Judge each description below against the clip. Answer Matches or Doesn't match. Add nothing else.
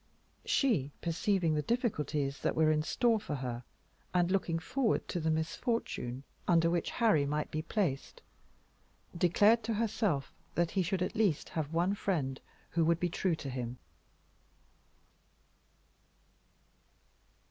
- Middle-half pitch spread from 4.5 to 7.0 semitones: Matches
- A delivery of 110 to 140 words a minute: Matches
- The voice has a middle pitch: Matches